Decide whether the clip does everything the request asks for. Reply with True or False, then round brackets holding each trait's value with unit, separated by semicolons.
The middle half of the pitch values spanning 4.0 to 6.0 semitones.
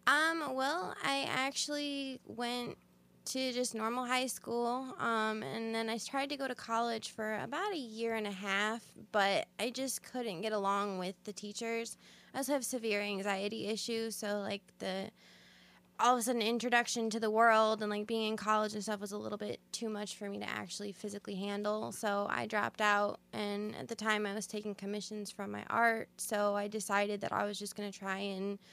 False (2.5 semitones)